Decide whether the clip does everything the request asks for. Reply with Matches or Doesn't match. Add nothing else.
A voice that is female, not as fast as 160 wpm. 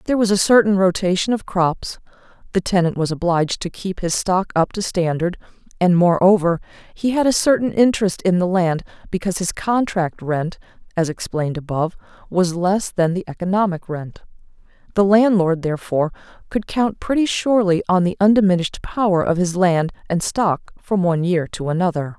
Doesn't match